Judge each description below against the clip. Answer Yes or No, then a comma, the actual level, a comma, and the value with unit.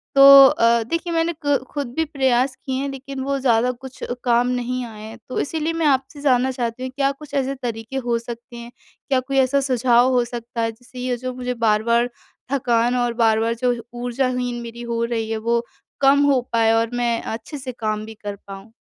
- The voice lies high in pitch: Yes, high, 245 Hz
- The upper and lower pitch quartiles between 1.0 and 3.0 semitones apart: Yes, narrow, 2.5 semitones